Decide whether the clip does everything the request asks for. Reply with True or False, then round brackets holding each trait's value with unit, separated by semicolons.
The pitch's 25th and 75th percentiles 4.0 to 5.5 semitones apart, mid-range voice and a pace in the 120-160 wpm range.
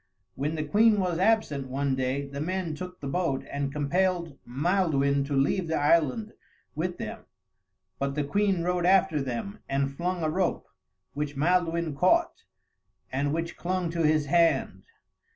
True (4.4 semitones; 160 Hz; 155 wpm)